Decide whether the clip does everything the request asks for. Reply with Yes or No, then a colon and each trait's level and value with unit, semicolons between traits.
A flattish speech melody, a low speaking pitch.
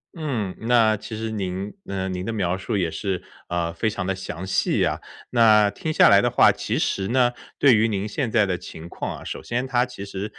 No: average, 3.4 semitones; low, 105 Hz